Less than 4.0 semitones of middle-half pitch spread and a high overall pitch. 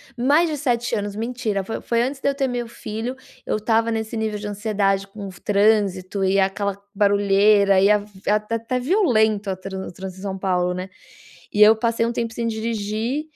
Yes: average, 2.7 semitones; high, 215 Hz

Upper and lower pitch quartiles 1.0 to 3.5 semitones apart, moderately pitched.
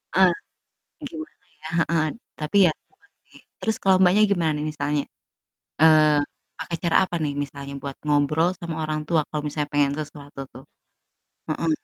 Yes: average, 2.8 semitones; medium, 155 Hz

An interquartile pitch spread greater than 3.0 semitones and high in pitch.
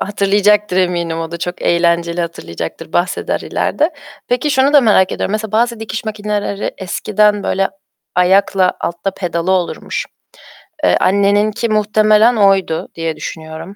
Yes: average, 3.7 semitones; high, 195 Hz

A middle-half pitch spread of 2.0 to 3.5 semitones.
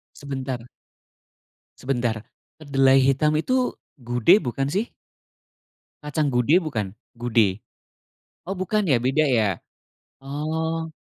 No: average, 4.3 semitones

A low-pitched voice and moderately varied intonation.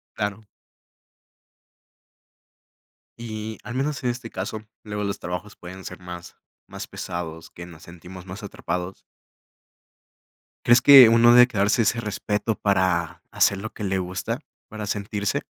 Yes: low, 100 Hz; average, 3.5 semitones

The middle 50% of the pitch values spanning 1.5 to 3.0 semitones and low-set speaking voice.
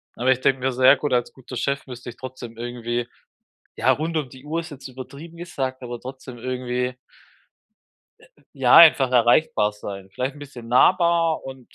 Yes: narrow, 2.5 semitones; low, 130 Hz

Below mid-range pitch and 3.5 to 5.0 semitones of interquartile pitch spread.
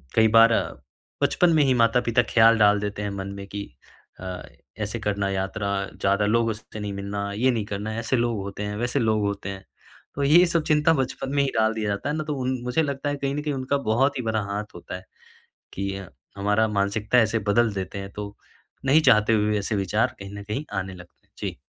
Yes: low, 110 Hz; average, 3.9 semitones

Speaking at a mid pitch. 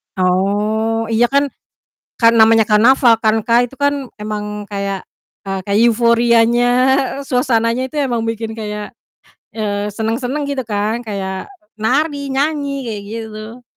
No: high, 225 Hz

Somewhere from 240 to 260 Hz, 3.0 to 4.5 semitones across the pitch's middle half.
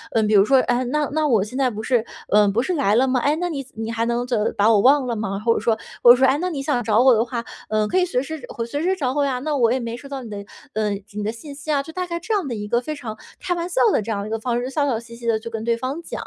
Yes: high, 245 Hz; average, 4.2 semitones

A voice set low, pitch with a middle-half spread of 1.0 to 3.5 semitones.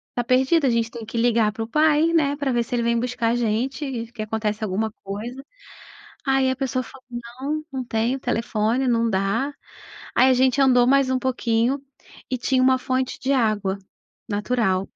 No: high, 245 Hz; average, 2.7 semitones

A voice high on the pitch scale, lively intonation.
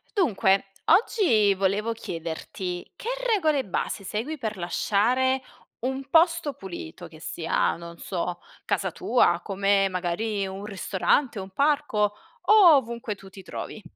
Yes: high, 210 Hz; wide, 5.8 semitones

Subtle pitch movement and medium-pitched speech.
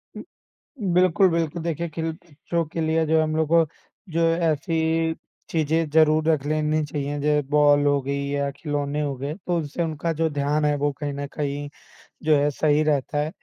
Yes: narrow, 1.9 semitones; medium, 155 Hz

